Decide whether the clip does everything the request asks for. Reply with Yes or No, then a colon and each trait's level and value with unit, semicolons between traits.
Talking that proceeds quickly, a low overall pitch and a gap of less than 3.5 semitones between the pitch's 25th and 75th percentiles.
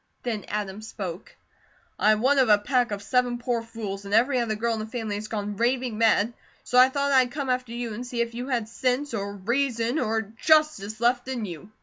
No: fast, 225 wpm; high, 230 Hz; average, 2.9 semitones